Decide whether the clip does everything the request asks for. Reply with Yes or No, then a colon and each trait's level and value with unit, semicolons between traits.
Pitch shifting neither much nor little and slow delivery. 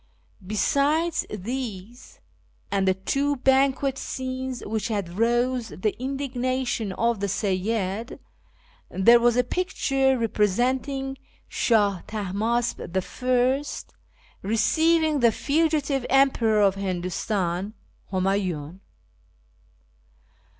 Yes: average, 5.0 semitones; slow, 85 wpm